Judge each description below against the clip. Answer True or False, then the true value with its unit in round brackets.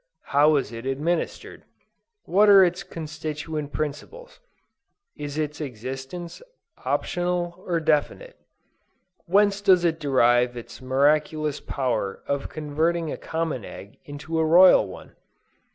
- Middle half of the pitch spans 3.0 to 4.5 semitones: True (3.6 semitones)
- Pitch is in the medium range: True (155 Hz)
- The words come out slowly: True (120 wpm)